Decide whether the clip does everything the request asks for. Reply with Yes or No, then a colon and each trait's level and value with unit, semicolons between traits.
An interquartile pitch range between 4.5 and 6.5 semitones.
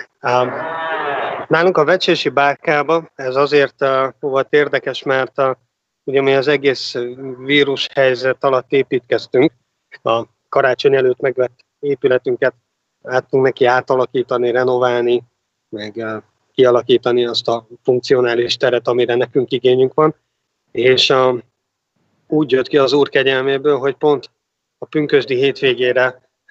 No: average, 2.9 semitones